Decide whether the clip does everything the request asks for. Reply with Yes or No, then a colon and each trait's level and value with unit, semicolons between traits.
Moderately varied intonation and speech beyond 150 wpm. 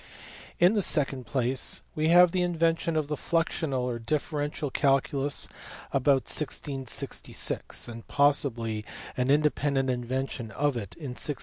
No: average, 3.3 semitones; slow, 135 wpm